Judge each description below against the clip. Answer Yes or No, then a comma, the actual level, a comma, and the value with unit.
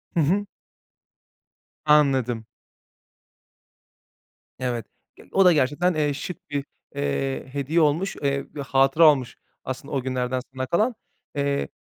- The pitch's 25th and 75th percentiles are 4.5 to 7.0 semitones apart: No, average, 3.0 semitones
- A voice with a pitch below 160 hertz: Yes, medium, 140 Hz